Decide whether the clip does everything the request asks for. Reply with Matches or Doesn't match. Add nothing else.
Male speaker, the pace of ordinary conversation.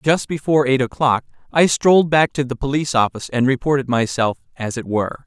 Matches